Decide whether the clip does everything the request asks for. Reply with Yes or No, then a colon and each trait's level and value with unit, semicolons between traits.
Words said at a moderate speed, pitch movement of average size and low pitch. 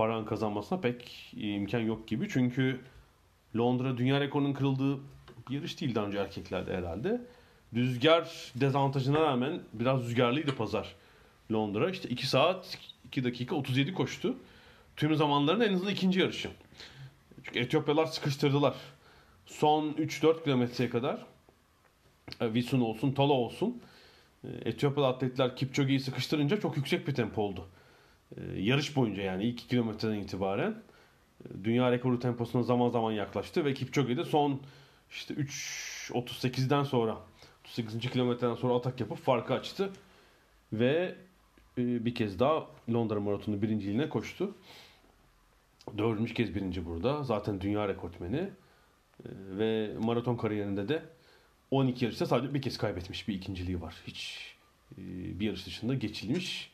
Yes: average, 125 wpm; average, 4.2 semitones; low, 125 Hz